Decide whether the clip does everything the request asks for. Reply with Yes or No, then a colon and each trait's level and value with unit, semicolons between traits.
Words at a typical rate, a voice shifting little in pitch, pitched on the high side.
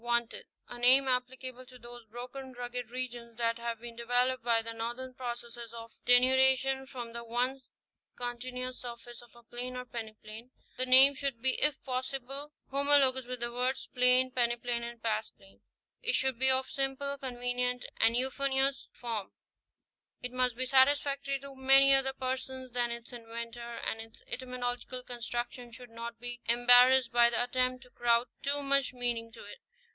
Yes: average, 165 wpm; narrow, 1.7 semitones; high, 245 Hz